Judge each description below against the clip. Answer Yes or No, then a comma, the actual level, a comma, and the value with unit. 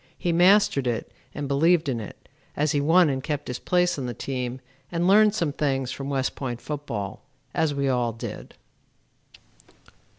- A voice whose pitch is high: No, medium, 140 Hz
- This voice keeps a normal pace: Yes, average, 170 wpm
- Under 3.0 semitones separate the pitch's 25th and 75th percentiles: No, average, 4.6 semitones